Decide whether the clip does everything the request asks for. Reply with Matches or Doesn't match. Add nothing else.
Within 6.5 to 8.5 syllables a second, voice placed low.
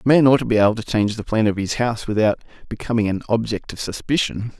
Matches